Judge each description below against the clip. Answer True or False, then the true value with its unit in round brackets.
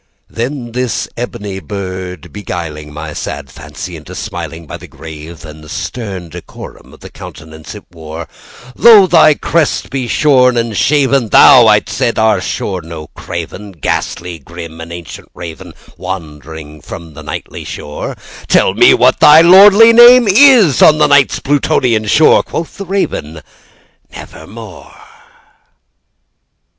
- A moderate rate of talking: False (125 wpm)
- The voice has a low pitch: True (100 Hz)